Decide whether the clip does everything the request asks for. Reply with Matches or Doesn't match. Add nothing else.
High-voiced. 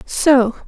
Matches